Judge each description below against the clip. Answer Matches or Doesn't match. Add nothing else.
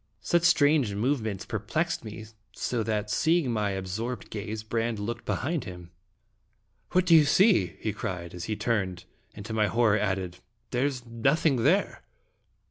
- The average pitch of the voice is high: Doesn't match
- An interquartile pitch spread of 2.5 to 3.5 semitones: Doesn't match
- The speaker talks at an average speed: Matches